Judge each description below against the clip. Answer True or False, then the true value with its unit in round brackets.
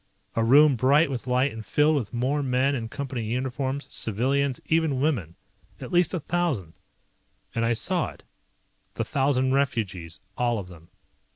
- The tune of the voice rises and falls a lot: False (3.6 semitones)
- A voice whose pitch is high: False (130 Hz)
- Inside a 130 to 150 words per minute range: False (160 wpm)